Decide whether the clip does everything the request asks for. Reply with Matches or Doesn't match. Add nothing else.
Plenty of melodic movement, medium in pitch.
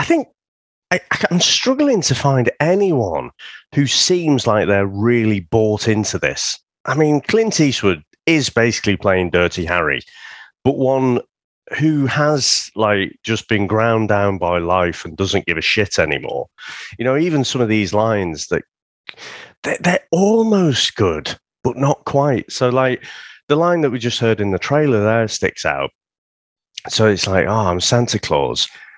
Doesn't match